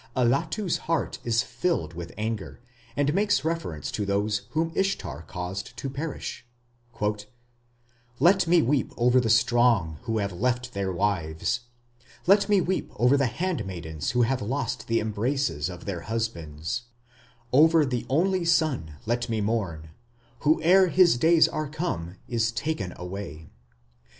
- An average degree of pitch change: No, wide, 8.0 semitones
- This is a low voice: Yes, low, 120 Hz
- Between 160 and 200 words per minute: No, average, 140 wpm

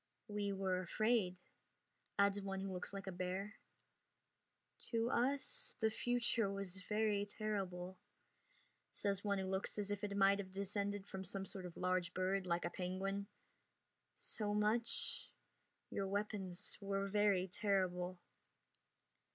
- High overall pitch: Yes, high, 195 Hz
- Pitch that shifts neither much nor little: No, narrow, 1.7 semitones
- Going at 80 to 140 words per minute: Yes, slow, 135 wpm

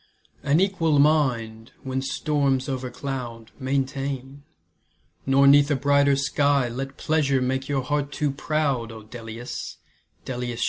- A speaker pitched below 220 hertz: Yes, low, 135 Hz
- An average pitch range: No, narrow, 2.2 semitones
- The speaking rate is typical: No, slow, 125 wpm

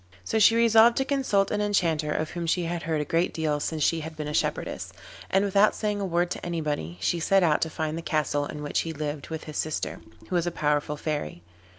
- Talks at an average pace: No, fast, 240 wpm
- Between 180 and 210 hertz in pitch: No, medium, 165 Hz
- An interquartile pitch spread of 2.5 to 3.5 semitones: No, average, 4.2 semitones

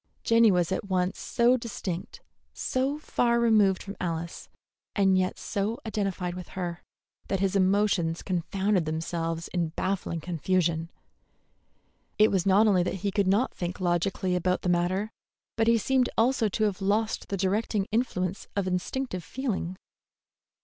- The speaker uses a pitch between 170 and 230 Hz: Yes, high, 190 Hz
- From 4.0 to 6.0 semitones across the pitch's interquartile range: No, average, 3.2 semitones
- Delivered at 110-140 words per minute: No, average, 150 wpm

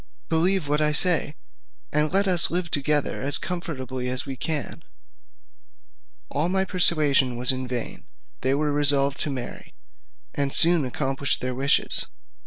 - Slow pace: No, average, 145 wpm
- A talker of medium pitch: Yes, medium, 145 Hz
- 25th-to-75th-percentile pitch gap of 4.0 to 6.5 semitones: No, average, 3.6 semitones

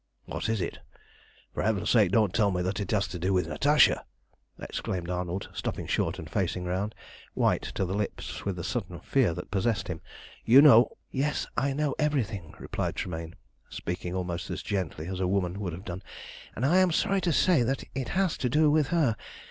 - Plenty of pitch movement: Yes, wide, 7.0 semitones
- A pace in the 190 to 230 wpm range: Yes, average, 200 wpm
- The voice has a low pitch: Yes, low, 100 Hz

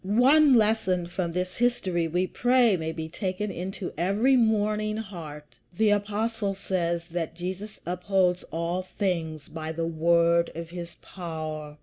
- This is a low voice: No, medium, 180 Hz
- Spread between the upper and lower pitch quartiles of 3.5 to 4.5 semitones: Yes, average, 3.8 semitones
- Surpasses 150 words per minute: No, average, 140 wpm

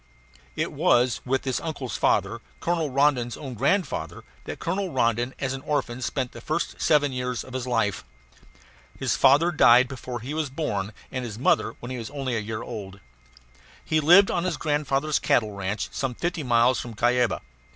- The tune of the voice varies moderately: Yes, average, 3.7 semitones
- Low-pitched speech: Yes, low, 130 Hz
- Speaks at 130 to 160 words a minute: No, average, 180 wpm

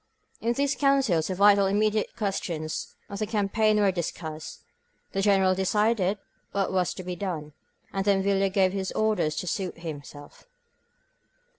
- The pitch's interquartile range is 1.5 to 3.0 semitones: Yes, average, 2.7 semitones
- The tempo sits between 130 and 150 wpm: No, average, 160 wpm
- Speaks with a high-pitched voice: Yes, high, 195 Hz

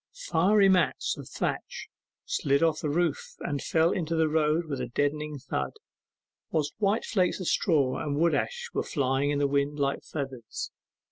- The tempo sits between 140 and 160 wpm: No, average, 175 wpm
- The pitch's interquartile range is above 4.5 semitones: No, average, 3.3 semitones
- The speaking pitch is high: No, medium, 150 Hz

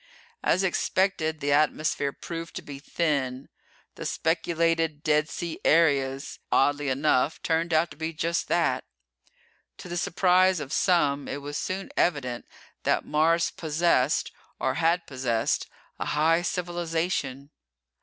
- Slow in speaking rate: Yes, slow, 130 wpm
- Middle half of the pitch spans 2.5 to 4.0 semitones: Yes, average, 2.9 semitones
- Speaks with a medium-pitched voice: Yes, medium, 160 Hz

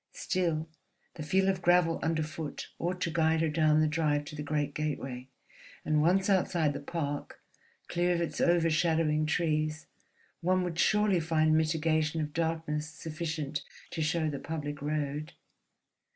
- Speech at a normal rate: Yes, average, 150 wpm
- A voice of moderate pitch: Yes, medium, 155 Hz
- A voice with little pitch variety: Yes, narrow, 1.8 semitones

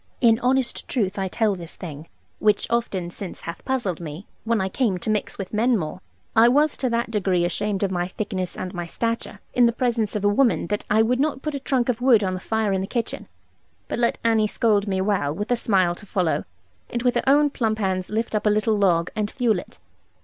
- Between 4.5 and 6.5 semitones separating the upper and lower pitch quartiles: No, average, 3.9 semitones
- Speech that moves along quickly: Yes, fast, 235 wpm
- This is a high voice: Yes, high, 210 Hz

